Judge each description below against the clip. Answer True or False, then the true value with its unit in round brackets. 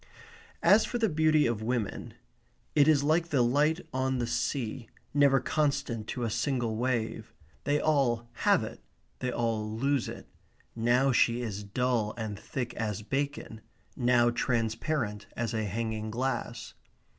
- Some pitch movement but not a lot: True (3.9 semitones)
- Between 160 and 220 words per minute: False (145 wpm)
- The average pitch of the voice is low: True (120 Hz)